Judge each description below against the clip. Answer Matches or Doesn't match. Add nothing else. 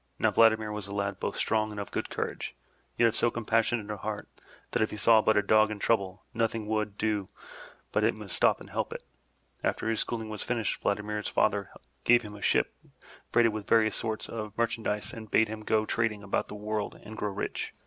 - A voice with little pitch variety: Matches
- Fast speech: Matches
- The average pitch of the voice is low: Matches